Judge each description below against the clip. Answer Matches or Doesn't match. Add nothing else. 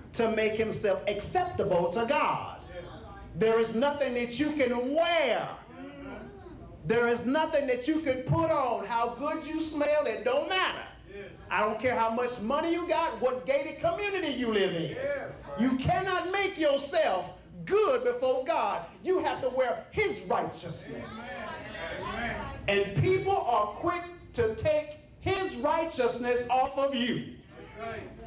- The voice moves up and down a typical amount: Doesn't match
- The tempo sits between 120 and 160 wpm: Matches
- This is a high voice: Matches